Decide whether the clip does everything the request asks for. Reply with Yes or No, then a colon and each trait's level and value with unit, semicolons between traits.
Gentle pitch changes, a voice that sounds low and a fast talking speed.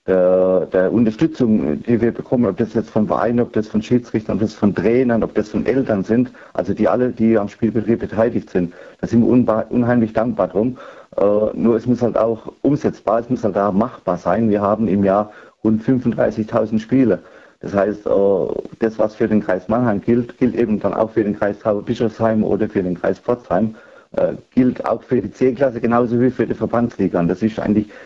Yes: narrow, 2.3 semitones; low, 110 Hz; fast, 200 wpm